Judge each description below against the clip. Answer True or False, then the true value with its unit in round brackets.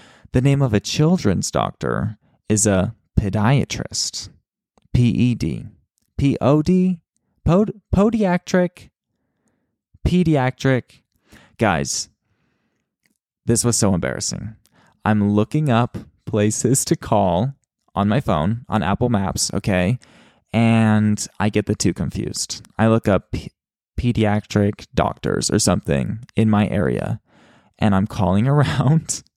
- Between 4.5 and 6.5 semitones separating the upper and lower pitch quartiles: True (4.8 semitones)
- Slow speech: True (110 wpm)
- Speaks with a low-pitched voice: True (110 Hz)